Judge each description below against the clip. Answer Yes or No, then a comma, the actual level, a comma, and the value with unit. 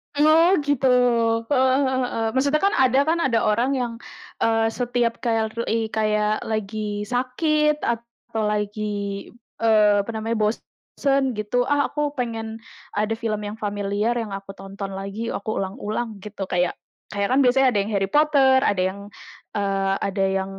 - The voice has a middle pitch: No, high, 225 Hz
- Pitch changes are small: No, average, 3.9 semitones